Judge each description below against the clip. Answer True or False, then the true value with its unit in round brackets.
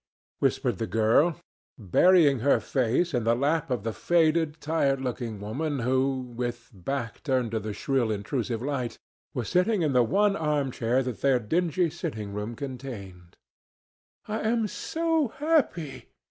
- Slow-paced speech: False (150 wpm)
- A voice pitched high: False (135 Hz)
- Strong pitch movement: True (5.8 semitones)